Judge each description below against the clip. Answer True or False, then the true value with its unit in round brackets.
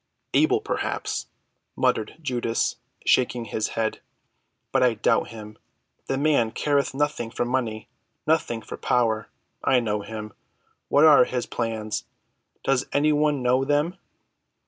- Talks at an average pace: False (125 wpm)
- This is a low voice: True (125 Hz)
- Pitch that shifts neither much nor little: True (4.2 semitones)